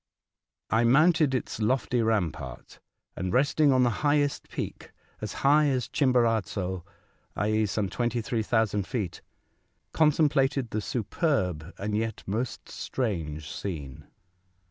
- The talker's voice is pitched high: No, low, 115 Hz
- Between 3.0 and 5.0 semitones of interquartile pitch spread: No, wide, 5.4 semitones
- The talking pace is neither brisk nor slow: No, slow, 110 wpm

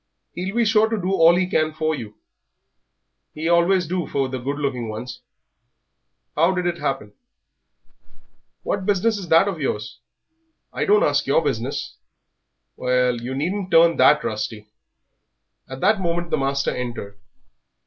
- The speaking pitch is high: No, medium, 155 Hz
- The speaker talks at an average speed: Yes, average, 155 wpm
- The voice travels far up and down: Yes, wide, 6.2 semitones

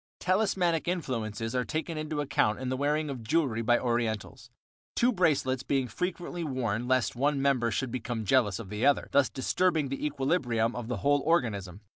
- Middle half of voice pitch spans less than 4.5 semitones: No, average, 4.8 semitones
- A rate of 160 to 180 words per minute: Yes, average, 175 wpm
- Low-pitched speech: Yes, low, 130 Hz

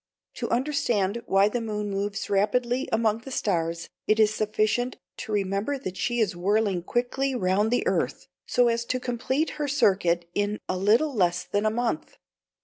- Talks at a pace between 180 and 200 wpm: No, average, 170 wpm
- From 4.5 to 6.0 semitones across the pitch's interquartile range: No, average, 3.7 semitones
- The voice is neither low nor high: No, high, 215 Hz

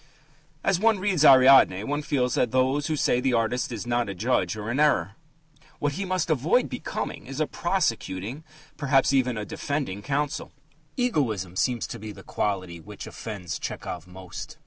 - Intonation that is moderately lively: No, wide, 6.0 semitones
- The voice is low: Yes, low, 130 Hz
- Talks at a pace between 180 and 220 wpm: No, average, 170 wpm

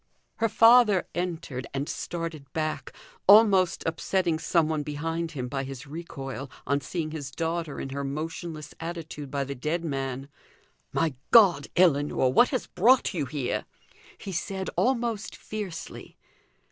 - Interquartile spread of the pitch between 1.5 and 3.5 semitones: No, average, 4.4 semitones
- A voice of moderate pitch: Yes, medium, 160 Hz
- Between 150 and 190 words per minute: No, average, 140 wpm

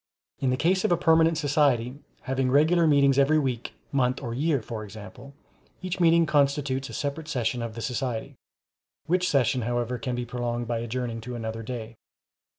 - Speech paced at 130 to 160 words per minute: No, average, 175 wpm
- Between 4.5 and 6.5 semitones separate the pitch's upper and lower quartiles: No, average, 3.9 semitones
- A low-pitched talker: Yes, low, 130 Hz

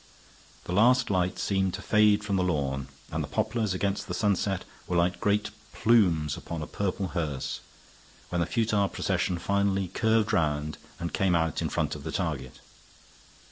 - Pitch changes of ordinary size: Yes, average, 3.4 semitones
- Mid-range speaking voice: No, very low, 95 Hz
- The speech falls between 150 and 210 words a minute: Yes, average, 170 wpm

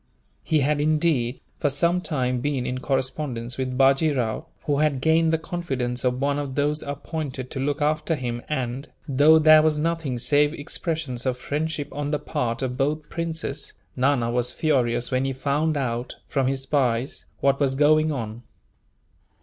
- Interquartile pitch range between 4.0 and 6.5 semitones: No, average, 3.2 semitones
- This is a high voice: No, medium, 140 Hz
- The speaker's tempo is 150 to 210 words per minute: Yes, average, 170 wpm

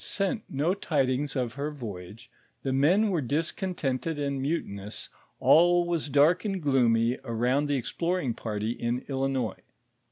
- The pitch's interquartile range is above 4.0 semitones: Yes, average, 5.3 semitones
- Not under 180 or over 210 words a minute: No, average, 140 wpm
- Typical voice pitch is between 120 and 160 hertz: Yes, medium, 140 Hz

